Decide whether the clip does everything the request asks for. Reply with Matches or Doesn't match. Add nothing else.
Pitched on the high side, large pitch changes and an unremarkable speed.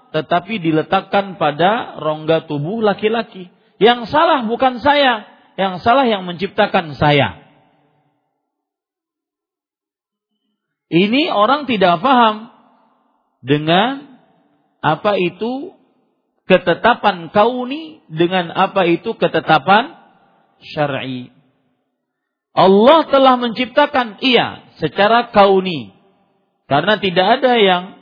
Doesn't match